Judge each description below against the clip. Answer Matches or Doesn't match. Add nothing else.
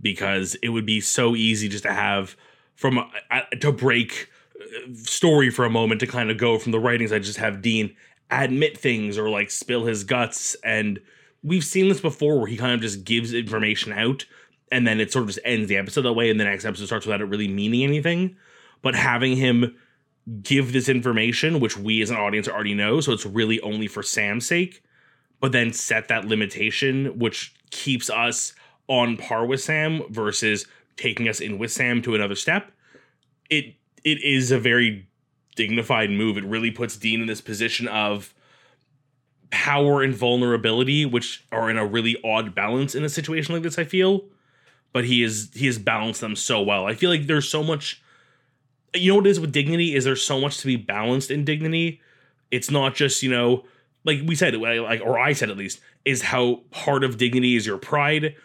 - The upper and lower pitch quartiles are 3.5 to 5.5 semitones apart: Matches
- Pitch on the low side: Matches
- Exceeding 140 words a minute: Matches